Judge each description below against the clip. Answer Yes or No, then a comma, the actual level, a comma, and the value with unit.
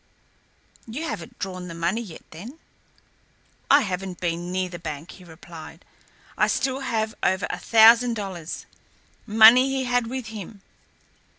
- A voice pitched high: Yes, high, 205 Hz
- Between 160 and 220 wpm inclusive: No, average, 140 wpm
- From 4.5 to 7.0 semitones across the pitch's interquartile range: Yes, wide, 5.4 semitones